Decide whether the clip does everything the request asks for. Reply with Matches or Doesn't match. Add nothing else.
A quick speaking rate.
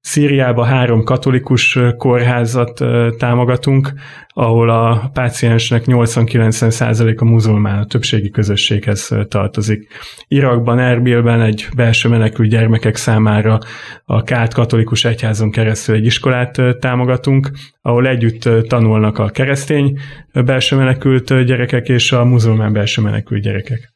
Doesn't match